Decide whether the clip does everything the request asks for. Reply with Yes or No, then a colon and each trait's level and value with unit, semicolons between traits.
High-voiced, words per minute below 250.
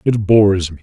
No: low, 100 Hz; fast, 220 wpm